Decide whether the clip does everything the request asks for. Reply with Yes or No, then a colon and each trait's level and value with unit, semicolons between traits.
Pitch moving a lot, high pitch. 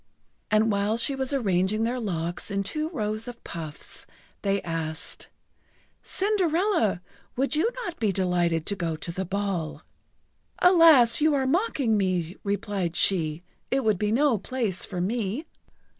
Yes: wide, 6.5 semitones; high, 210 Hz